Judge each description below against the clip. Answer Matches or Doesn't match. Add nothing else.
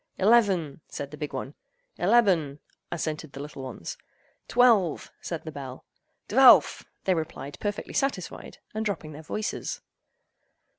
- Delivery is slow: Matches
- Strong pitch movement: Matches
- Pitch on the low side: Doesn't match